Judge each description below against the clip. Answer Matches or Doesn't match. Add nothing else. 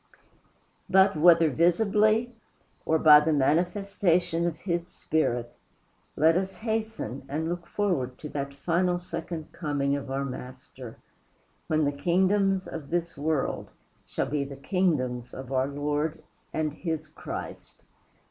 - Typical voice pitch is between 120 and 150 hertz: Doesn't match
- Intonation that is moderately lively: Matches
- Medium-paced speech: Doesn't match